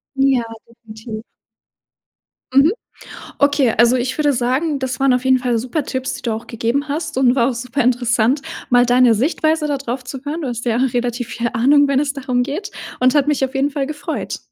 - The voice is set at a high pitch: Yes, very high, 260 Hz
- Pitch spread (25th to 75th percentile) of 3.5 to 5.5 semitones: No, average, 2.7 semitones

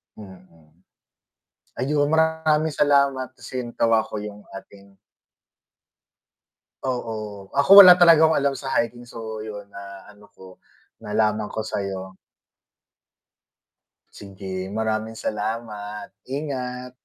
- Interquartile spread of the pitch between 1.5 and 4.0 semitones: No, average, 4.9 semitones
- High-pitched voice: No, low, 110 Hz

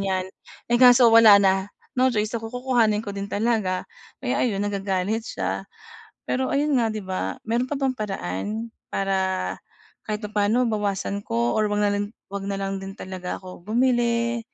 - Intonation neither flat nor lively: Yes, average, 3.1 semitones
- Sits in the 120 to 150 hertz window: No, high, 210 Hz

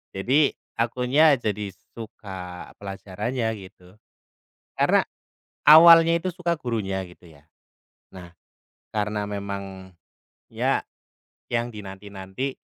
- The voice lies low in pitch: Yes, low, 105 Hz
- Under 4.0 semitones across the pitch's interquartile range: No, average, 4.6 semitones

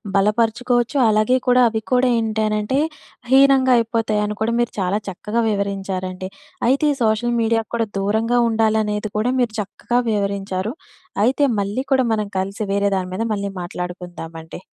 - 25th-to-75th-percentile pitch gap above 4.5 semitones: No, average, 2.9 semitones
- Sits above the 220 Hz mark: No, high, 215 Hz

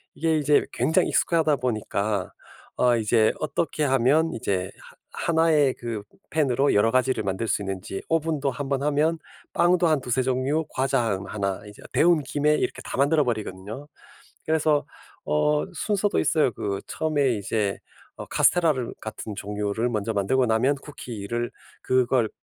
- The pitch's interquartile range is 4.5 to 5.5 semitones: No, wide, 5.9 semitones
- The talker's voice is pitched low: Yes, low, 130 Hz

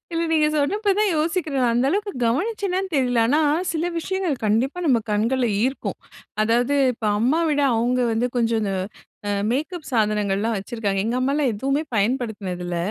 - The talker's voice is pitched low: No, very high, 255 Hz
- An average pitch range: No, wide, 5.8 semitones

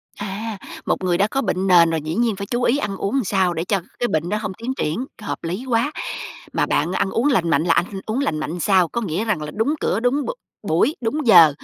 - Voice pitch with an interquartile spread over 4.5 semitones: Yes, wide, 5.4 semitones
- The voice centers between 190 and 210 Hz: Yes, high, 200 Hz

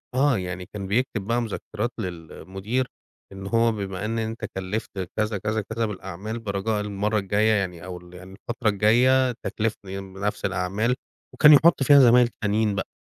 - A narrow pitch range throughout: No, average, 3.1 semitones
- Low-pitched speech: Yes, low, 105 Hz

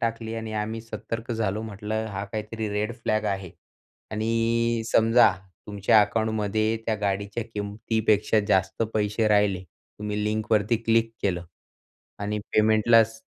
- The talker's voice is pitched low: Yes, low, 110 Hz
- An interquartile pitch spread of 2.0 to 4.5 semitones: No, narrow, 1.4 semitones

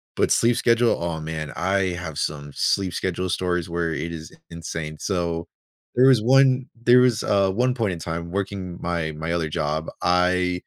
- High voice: No, very low, 90 Hz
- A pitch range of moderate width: Yes, average, 3.6 semitones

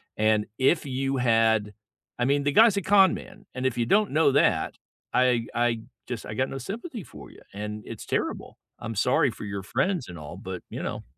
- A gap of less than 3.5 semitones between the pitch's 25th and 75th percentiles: No, average, 5.1 semitones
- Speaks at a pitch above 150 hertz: No, low, 125 Hz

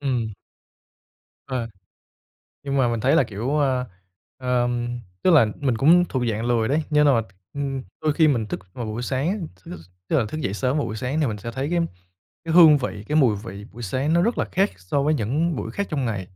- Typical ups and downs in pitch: Yes, average, 4.7 semitones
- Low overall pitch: Yes, low, 130 Hz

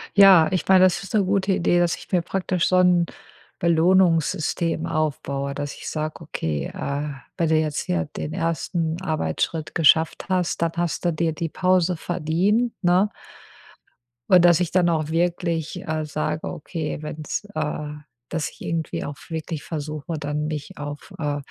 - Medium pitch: Yes, medium, 165 Hz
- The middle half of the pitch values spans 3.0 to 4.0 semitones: No, narrow, 2.6 semitones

